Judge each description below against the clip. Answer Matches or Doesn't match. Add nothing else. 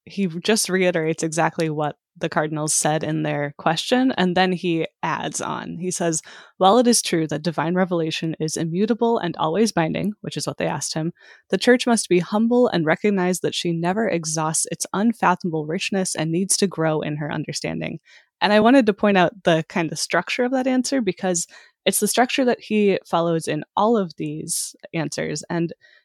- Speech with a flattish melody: Doesn't match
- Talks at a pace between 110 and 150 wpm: Doesn't match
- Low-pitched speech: Doesn't match